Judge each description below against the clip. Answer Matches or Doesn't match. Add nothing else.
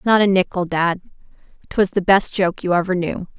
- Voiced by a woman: Matches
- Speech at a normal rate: Matches